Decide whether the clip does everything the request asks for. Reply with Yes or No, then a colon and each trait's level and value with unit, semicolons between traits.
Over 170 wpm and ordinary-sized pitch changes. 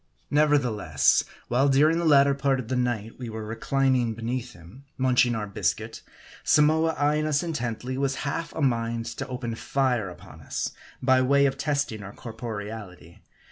No: average, 160 wpm; average, 3.6 semitones